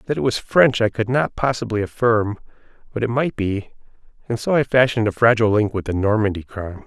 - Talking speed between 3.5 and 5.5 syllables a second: No, 6.1 syllables/s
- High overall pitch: No, low, 110 Hz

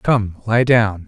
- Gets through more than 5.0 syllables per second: No, 3.3 syllables/s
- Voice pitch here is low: Yes, low, 105 Hz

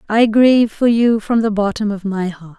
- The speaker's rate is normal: No, fast, 230 wpm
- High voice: Yes, high, 215 Hz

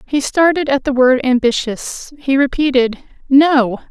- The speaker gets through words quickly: No, average, 140 wpm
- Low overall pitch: No, very high, 270 Hz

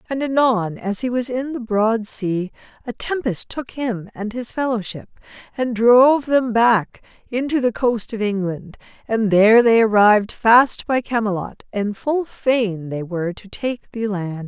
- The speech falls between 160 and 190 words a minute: Yes, average, 170 wpm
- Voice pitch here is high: Yes, high, 225 Hz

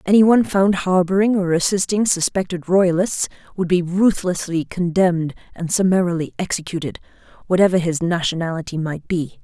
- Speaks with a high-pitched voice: No, medium, 180 Hz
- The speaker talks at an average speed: No, slow, 120 wpm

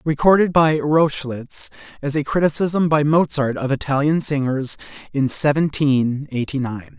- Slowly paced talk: Yes, slow, 130 wpm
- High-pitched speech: No, medium, 145 Hz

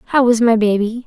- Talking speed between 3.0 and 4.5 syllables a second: No, 4.9 syllables/s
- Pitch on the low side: No, high, 230 Hz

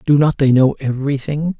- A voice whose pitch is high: No, medium, 140 Hz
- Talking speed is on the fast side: No, average, 190 wpm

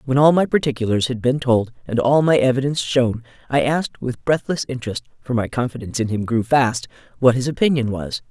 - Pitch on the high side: No, low, 125 Hz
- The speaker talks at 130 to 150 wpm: No, average, 190 wpm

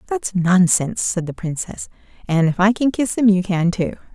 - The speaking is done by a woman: Yes, female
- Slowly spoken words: No, fast, 205 wpm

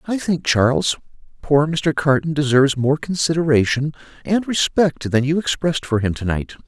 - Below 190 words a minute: Yes, average, 160 wpm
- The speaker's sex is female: No, male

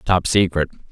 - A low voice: Yes, very low, 90 Hz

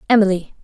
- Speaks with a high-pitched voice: Yes, high, 200 Hz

